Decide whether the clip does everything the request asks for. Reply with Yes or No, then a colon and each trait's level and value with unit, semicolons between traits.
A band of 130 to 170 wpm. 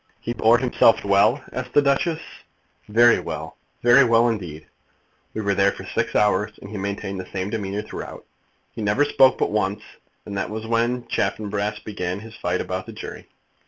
No: average, 180 wpm